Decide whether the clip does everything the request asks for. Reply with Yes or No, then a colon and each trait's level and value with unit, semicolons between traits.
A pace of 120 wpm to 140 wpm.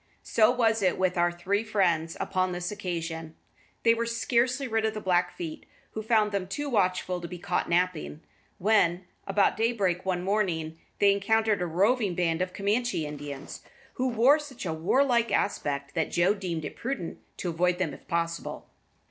No: average, 175 wpm